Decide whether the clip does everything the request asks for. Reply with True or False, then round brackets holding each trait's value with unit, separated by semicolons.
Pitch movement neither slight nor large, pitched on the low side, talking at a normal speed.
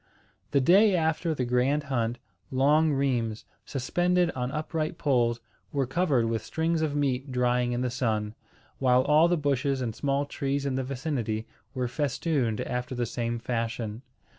True (3.5 semitones; 130 Hz; 160 wpm)